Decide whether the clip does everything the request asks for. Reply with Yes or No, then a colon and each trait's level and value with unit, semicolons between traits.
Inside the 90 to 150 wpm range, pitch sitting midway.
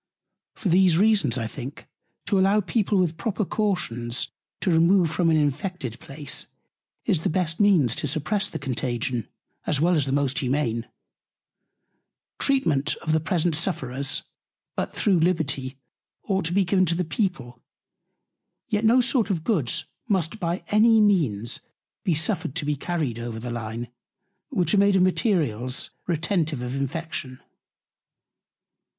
Yes: average, 145 wpm; medium, 165 Hz